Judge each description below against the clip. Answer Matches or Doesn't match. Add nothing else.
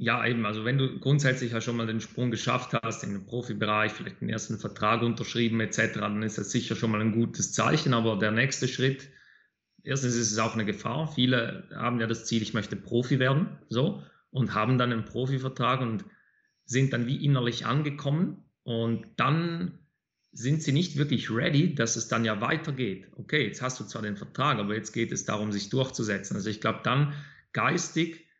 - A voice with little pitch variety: Doesn't match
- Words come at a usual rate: Doesn't match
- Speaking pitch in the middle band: Doesn't match